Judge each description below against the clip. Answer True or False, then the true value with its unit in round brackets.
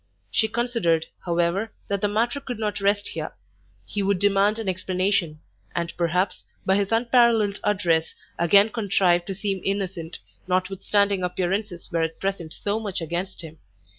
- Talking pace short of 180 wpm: True (150 wpm)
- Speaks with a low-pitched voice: False (195 Hz)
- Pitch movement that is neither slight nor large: True (3.0 semitones)